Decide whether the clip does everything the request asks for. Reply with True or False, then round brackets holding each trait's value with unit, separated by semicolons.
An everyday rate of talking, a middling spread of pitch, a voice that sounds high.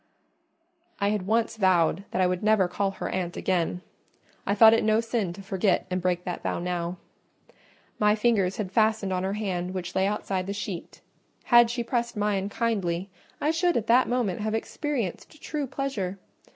True (180 wpm; 3.7 semitones; 200 Hz)